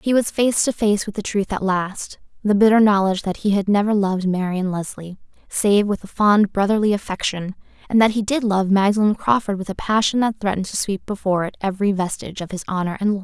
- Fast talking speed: Yes, fast, 220 wpm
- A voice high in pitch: Yes, high, 200 Hz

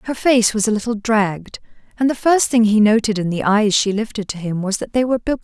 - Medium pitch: No, high, 220 Hz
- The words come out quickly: Yes, fast, 265 wpm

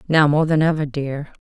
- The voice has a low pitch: No, medium, 150 Hz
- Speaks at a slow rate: No, fast, 210 wpm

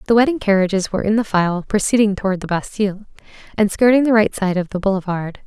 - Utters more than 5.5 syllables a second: Yes, 6.5 syllables/s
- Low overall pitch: No, high, 200 Hz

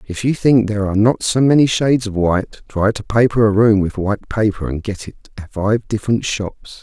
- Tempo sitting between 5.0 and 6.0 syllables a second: Yes, 5.5 syllables/s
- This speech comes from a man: Yes, male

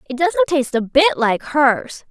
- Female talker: Yes, female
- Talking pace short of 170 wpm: No, average, 200 wpm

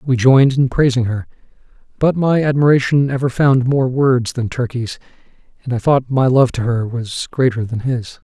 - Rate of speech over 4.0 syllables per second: Yes, 4.9 syllables/s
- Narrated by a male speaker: Yes, male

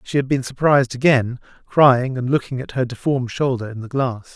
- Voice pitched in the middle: No, low, 130 Hz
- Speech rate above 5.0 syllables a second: Yes, 5.5 syllables/s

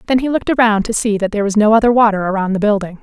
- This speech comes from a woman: Yes, female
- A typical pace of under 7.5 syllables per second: No, 7.9 syllables/s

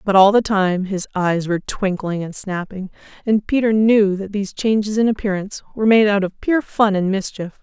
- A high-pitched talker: Yes, high, 200 Hz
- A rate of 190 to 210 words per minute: Yes, fast, 205 wpm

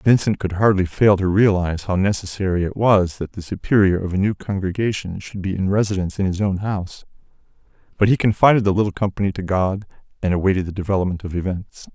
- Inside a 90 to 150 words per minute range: No, average, 195 wpm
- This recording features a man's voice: Yes, male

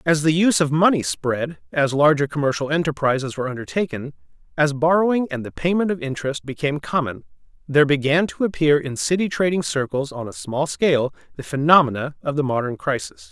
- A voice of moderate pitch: Yes, medium, 145 Hz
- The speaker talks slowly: No, average, 175 wpm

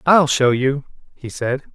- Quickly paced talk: No, average, 170 wpm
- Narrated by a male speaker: Yes, male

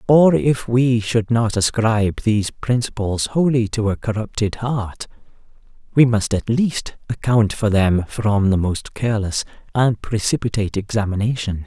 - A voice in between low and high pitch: No, low, 110 Hz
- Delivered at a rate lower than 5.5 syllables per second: Yes, 4.5 syllables/s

